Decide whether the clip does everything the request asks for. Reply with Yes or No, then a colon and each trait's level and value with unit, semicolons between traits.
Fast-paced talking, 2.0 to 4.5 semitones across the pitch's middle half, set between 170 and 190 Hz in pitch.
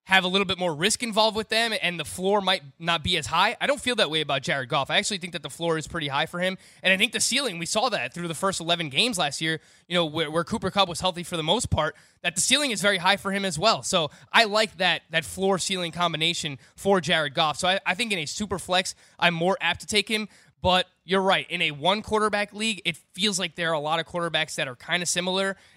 Yes: fast, 280 wpm; average, 2.9 semitones; medium, 185 Hz